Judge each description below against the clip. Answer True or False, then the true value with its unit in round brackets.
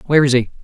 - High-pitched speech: False (135 Hz)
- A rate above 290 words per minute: False (285 wpm)